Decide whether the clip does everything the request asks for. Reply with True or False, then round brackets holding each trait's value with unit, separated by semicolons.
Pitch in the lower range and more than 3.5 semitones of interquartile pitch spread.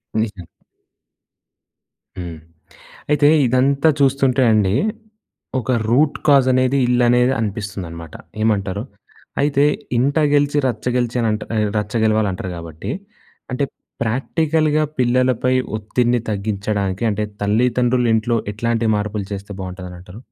True (115 Hz; 4.0 semitones)